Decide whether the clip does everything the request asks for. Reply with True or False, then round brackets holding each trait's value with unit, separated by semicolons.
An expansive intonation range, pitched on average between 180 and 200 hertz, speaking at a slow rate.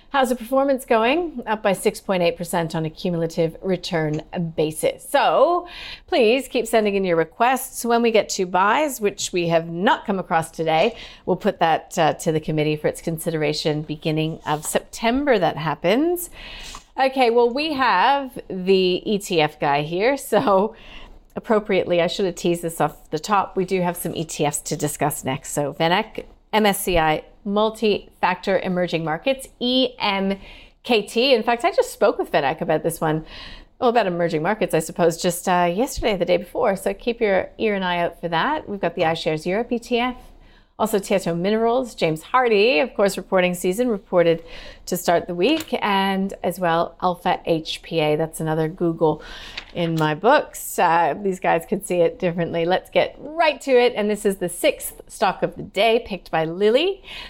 False (5.7 semitones; 185 Hz; 175 wpm)